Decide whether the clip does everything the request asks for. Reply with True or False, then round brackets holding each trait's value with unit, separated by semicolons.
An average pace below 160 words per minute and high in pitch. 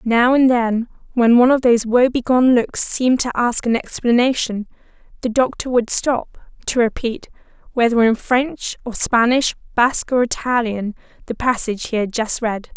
True (150 wpm; 240 Hz)